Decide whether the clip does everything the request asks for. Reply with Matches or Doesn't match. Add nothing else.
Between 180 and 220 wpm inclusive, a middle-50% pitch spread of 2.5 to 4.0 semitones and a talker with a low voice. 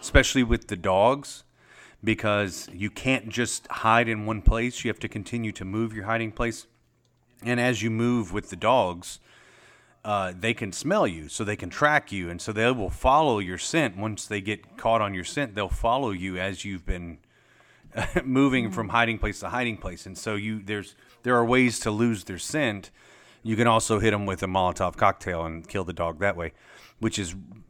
Matches